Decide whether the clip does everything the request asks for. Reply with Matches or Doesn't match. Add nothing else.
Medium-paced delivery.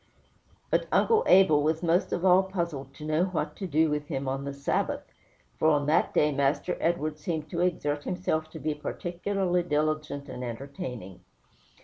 Matches